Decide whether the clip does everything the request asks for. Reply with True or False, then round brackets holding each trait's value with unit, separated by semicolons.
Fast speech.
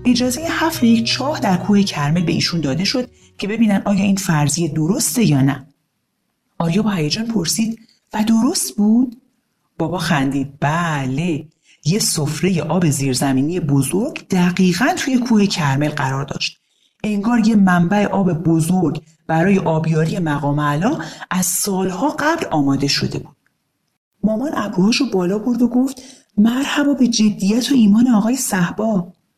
False (140 wpm)